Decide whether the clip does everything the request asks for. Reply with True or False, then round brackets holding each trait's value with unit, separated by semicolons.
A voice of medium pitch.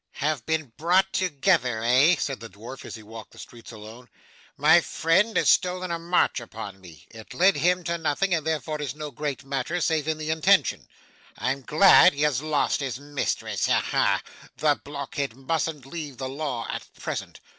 True (145 Hz)